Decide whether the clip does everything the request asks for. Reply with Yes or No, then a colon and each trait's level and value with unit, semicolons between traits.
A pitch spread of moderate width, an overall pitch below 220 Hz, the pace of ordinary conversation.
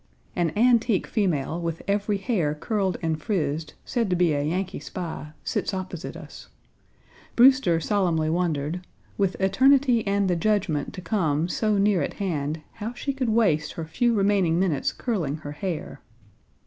Yes: average, 4.7 semitones; medium, 185 Hz; average, 155 wpm